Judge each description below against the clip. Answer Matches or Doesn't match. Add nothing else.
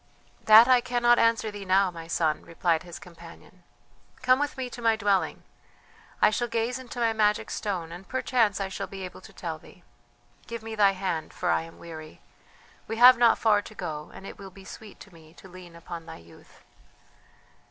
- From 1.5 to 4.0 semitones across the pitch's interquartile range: Doesn't match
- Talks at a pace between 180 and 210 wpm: Matches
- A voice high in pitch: Matches